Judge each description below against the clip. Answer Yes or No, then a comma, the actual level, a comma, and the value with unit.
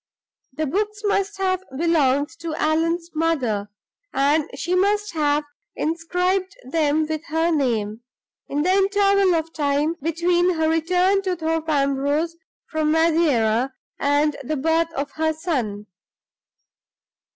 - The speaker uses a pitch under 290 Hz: No, very high, 320 Hz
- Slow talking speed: Yes, slow, 125 wpm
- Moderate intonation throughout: Yes, average, 3.4 semitones